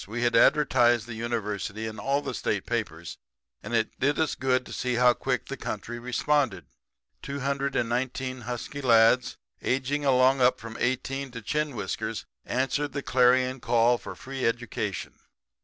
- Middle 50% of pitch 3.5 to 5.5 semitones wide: No, narrow, 2.5 semitones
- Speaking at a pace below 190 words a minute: Yes, average, 165 wpm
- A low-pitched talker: Yes, low, 125 Hz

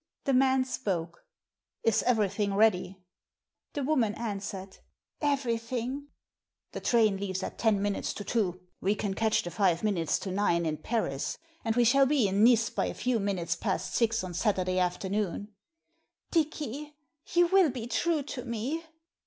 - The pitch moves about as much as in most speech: Yes, average, 4.8 semitones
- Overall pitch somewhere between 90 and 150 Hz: No, high, 220 Hz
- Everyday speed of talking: Yes, average, 170 wpm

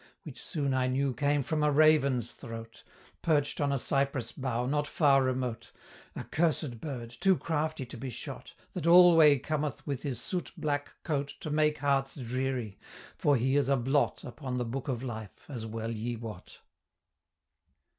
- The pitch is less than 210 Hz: Yes, low, 135 Hz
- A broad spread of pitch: No, average, 3.3 semitones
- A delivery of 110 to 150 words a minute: No, average, 170 wpm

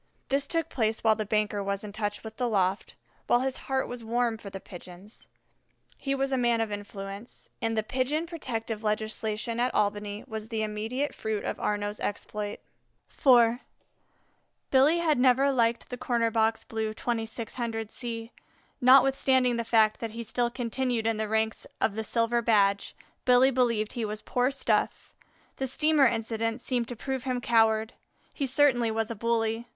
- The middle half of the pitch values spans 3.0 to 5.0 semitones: No, narrow, 2.5 semitones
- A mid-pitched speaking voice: No, high, 230 Hz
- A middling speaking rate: Yes, average, 170 wpm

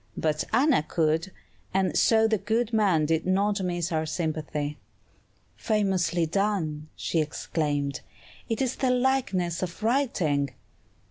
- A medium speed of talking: No, slow, 125 wpm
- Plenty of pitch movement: Yes, wide, 5.7 semitones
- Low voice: No, medium, 180 Hz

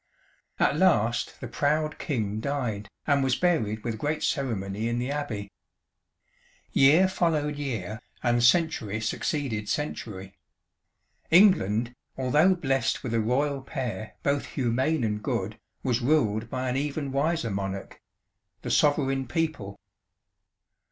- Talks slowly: Yes, slow, 125 wpm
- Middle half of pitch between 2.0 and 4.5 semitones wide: No, average, 5.2 semitones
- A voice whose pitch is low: Yes, low, 130 Hz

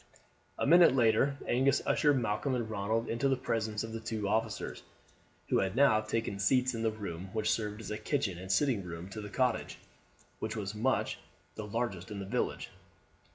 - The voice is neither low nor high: No, low, 110 Hz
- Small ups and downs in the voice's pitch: No, average, 3.3 semitones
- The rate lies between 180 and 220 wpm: Yes, average, 185 wpm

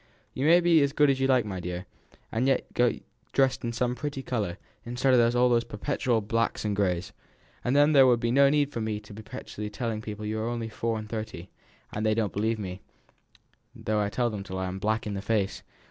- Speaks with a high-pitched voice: No, low, 115 Hz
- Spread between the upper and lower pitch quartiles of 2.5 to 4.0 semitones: Yes, average, 3.4 semitones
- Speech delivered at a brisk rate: Yes, fast, 235 wpm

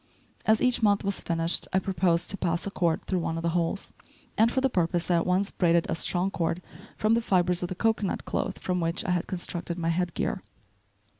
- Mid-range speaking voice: Yes, medium, 180 Hz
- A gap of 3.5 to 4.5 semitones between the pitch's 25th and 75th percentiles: No, average, 2.7 semitones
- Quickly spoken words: Yes, fast, 225 wpm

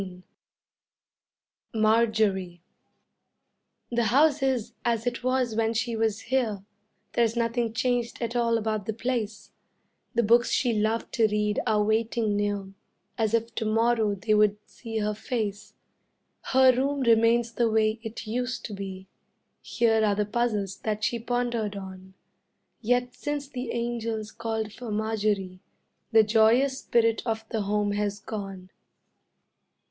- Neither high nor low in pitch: No, high, 225 Hz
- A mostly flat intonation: Yes, narrow, 2.1 semitones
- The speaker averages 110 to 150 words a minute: Yes, average, 140 wpm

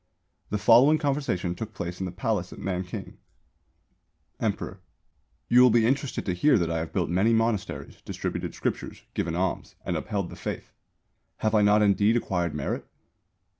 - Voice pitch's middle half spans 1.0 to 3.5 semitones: No, average, 4.3 semitones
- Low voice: Yes, low, 105 Hz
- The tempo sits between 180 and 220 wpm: No, average, 165 wpm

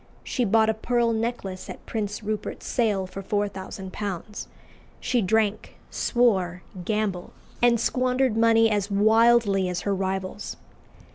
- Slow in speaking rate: Yes, slow, 125 wpm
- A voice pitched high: Yes, high, 210 Hz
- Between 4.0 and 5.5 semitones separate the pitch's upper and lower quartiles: No, average, 3.0 semitones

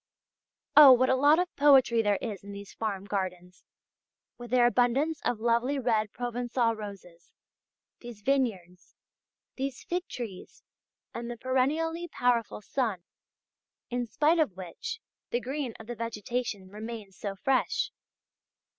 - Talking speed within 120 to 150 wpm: Yes, slow, 135 wpm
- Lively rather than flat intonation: No, average, 4.3 semitones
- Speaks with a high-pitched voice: Yes, high, 240 Hz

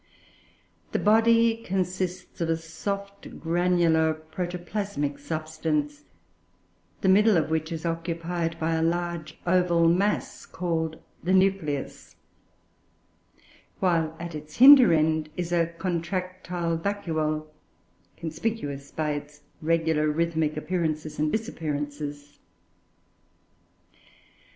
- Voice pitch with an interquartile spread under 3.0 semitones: Yes, narrow, 2.6 semitones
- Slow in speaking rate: Yes, slow, 100 wpm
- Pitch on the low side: No, medium, 165 Hz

